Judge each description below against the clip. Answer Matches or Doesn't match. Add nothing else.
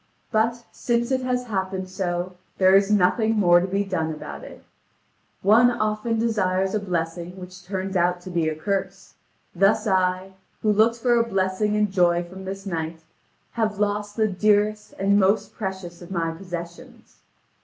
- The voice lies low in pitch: Doesn't match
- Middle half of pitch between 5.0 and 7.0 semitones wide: Doesn't match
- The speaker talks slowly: Doesn't match